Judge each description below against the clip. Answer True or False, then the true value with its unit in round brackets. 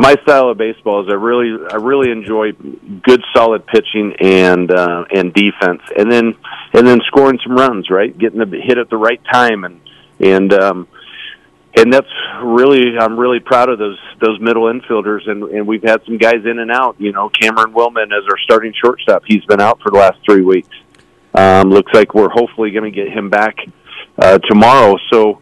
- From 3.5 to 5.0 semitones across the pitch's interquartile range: False (2.9 semitones)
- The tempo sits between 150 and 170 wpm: False (200 wpm)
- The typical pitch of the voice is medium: False (110 Hz)